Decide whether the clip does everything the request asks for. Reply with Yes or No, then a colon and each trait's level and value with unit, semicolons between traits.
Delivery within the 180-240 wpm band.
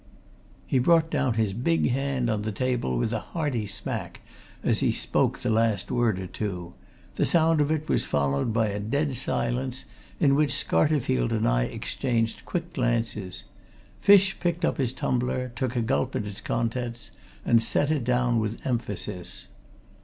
No: average, 170 wpm